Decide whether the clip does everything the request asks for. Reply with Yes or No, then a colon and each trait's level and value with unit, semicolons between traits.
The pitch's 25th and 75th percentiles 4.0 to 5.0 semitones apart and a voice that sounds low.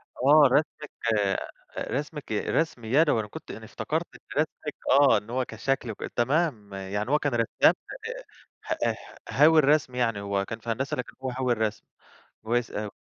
Yes: average, 4.7 semitones; low, 125 Hz